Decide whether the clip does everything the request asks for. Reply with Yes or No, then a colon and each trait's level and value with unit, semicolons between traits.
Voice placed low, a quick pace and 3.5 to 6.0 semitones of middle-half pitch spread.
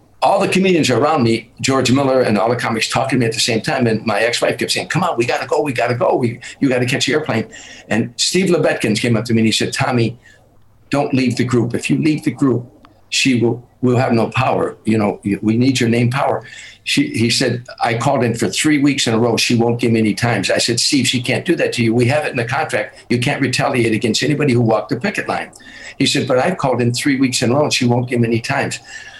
No: low, 125 Hz; fast, 270 wpm; average, 3.1 semitones